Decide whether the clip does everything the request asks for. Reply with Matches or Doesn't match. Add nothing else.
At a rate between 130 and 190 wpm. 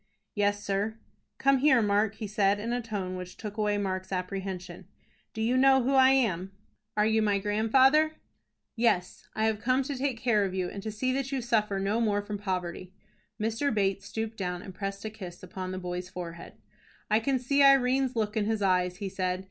Doesn't match